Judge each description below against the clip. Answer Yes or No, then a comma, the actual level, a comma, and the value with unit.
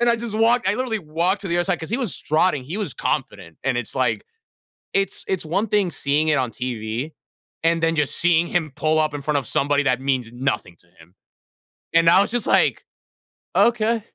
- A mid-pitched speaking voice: Yes, medium, 160 Hz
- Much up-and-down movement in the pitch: Yes, wide, 6.5 semitones